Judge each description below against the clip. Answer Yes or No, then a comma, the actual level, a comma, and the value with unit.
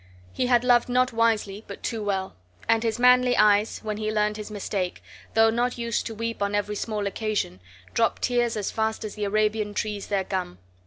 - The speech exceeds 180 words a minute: Yes, average, 200 wpm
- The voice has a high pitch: Yes, high, 215 Hz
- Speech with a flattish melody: Yes, narrow, 2.0 semitones